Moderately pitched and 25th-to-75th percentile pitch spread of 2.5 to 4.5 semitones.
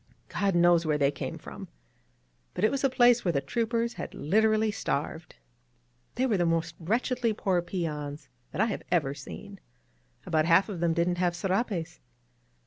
No: medium, 175 Hz; average, 5.2 semitones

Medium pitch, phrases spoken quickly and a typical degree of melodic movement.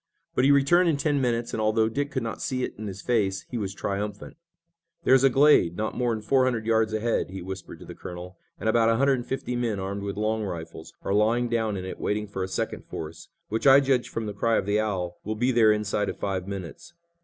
No: low, 110 Hz; fast, 245 wpm; average, 3.7 semitones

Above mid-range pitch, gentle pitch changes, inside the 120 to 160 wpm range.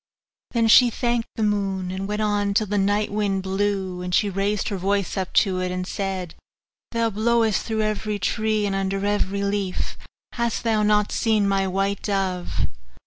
No: high, 200 Hz; narrow, 1.7 semitones; average, 180 wpm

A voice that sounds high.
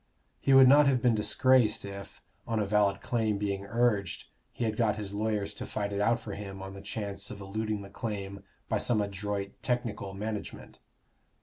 No: low, 105 Hz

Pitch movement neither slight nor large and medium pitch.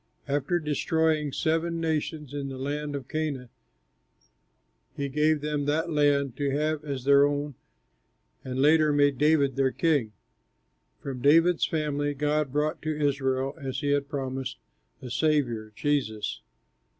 No: narrow, 2.0 semitones; medium, 145 Hz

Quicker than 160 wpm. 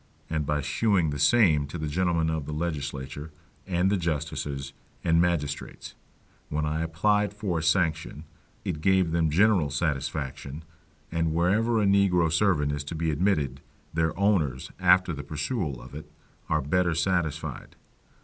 No: average, 150 wpm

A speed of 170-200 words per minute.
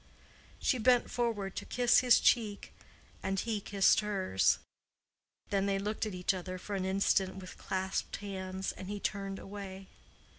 No: average, 155 wpm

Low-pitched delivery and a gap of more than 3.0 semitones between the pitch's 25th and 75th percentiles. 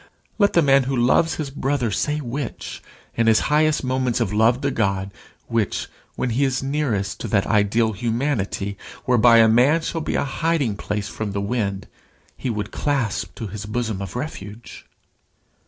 Yes: low, 120 Hz; average, 4.7 semitones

